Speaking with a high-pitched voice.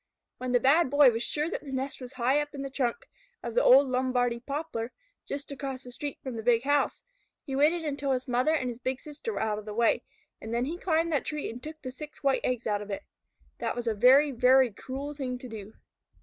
Yes: very high, 260 Hz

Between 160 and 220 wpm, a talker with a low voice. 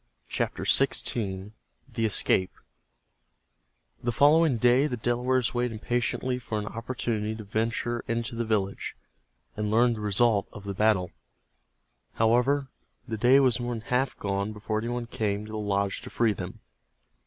No: average, 150 wpm; low, 115 Hz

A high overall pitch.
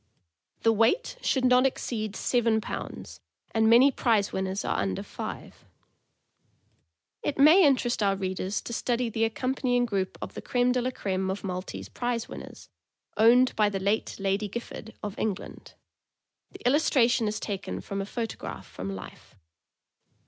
Yes: high, 225 Hz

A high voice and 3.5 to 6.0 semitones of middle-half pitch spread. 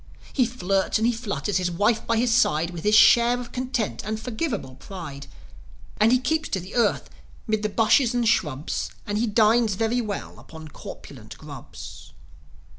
Yes: high, 220 Hz; average, 3.9 semitones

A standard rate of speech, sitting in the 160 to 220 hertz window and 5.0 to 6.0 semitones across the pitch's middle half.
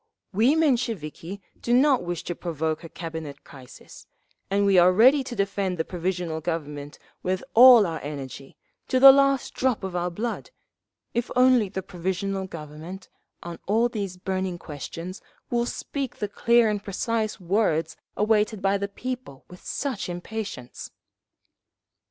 Yes: average, 145 wpm; high, 190 Hz; average, 5.3 semitones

